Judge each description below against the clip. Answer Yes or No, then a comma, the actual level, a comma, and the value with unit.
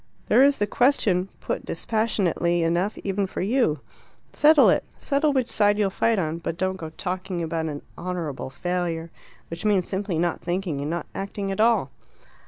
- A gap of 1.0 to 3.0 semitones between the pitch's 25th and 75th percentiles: No, average, 3.8 semitones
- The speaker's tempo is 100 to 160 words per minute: No, average, 175 wpm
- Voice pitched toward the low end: No, medium, 185 Hz